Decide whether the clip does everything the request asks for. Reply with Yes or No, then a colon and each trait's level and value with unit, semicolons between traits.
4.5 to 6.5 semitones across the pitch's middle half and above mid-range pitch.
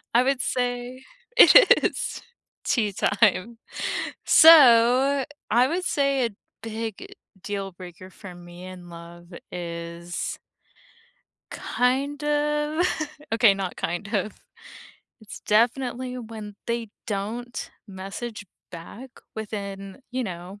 Yes: average, 5.0 semitones; high, 220 Hz